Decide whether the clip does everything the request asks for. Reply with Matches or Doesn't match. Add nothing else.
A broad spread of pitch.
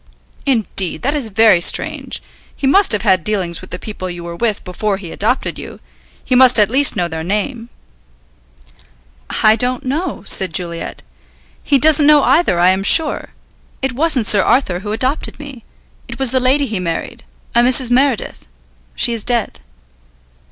Matches